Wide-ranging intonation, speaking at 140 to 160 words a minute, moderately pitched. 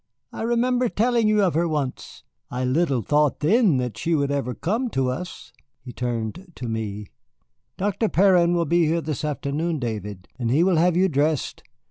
No: wide, 6.4 semitones; average, 180 wpm; medium, 155 Hz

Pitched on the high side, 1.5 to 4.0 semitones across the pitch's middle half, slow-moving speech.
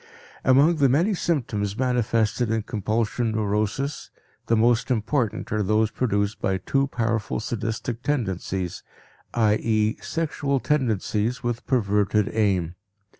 No: low, 115 Hz; average, 3.3 semitones; slow, 115 wpm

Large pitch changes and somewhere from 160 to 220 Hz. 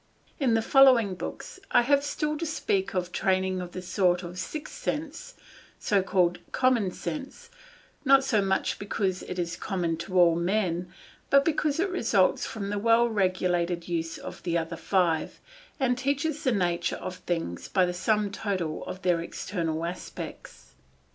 Yes: wide, 6.4 semitones; high, 190 Hz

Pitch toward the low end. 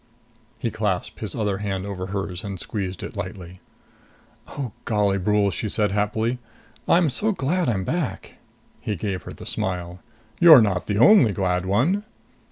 Yes: low, 105 Hz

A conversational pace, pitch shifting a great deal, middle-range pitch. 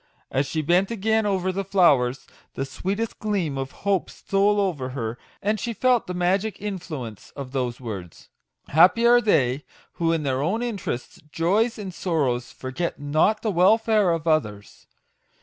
Yes: average, 160 wpm; wide, 7.2 semitones; medium, 175 Hz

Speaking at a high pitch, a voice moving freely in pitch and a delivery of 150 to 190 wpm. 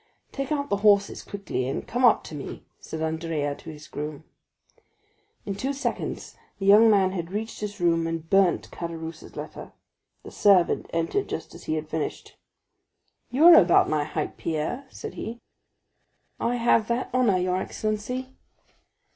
Yes: high, 195 Hz; wide, 5.8 semitones; average, 160 wpm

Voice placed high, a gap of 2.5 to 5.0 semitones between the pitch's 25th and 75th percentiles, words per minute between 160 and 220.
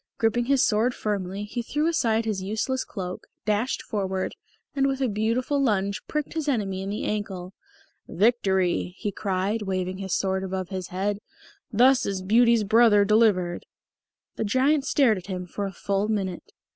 Yes: high, 210 Hz; average, 3.8 semitones; average, 170 wpm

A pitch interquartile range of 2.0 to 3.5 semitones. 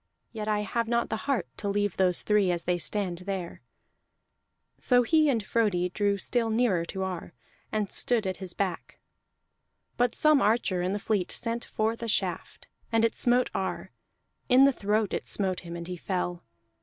No: average, 3.9 semitones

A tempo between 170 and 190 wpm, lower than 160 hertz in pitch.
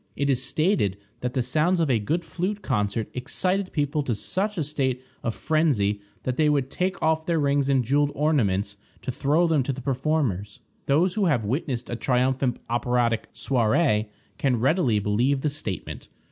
Yes: average, 175 wpm; low, 135 Hz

